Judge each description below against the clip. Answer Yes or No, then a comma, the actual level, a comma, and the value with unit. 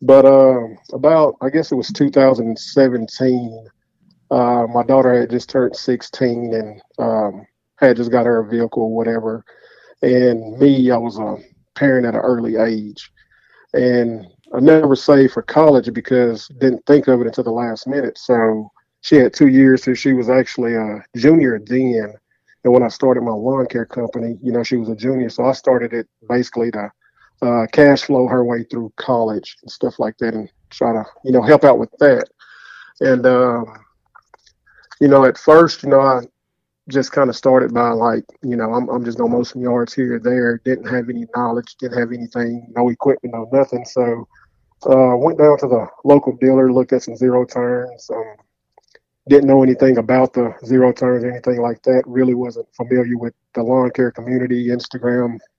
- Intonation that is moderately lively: No, narrow, 1.8 semitones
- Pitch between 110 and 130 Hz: Yes, low, 125 Hz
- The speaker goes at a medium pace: Yes, average, 185 wpm